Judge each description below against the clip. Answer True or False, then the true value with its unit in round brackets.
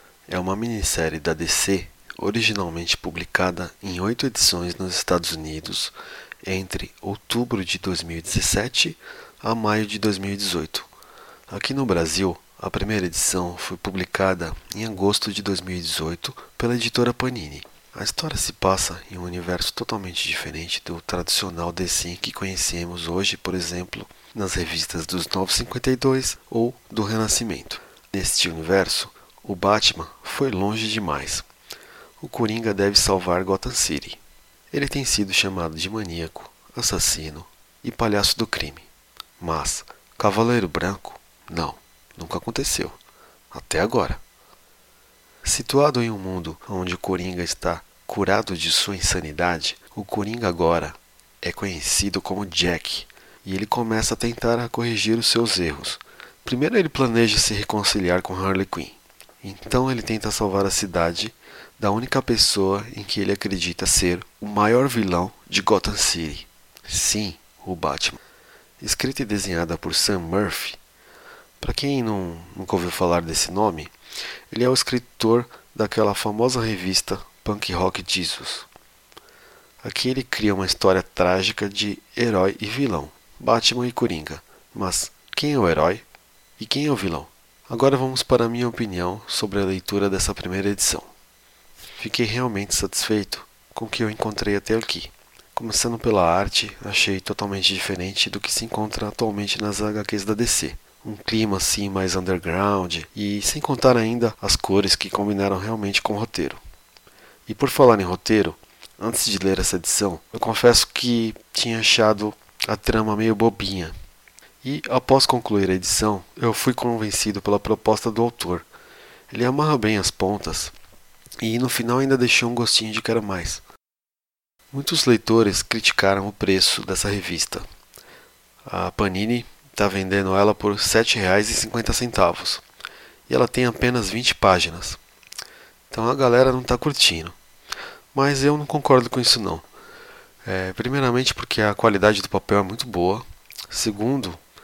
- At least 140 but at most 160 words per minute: True (145 wpm)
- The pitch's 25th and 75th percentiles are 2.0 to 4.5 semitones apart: True (3.9 semitones)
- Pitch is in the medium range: False (100 Hz)